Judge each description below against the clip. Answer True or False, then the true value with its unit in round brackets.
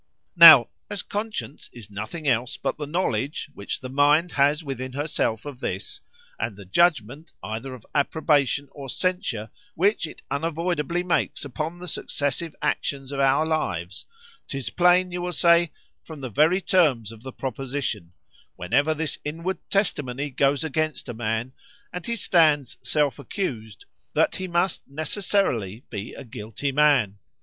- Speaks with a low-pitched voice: False (145 Hz)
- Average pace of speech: True (150 wpm)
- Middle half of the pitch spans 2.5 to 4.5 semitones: False (5.2 semitones)